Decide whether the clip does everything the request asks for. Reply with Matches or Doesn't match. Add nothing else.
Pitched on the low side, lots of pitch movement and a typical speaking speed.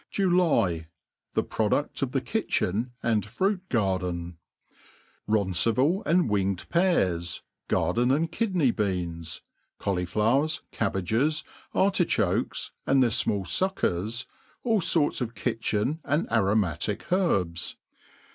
Doesn't match